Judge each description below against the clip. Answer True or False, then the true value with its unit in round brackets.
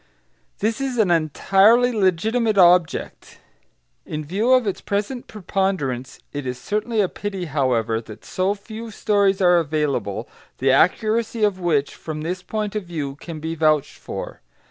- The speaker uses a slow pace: False (150 wpm)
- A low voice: False (185 Hz)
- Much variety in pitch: True (5.8 semitones)